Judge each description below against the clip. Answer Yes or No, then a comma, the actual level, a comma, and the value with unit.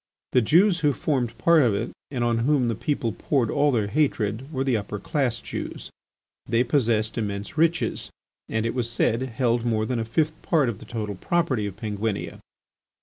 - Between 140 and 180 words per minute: No, average, 190 wpm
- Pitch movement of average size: Yes, average, 4.5 semitones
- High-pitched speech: No, low, 120 Hz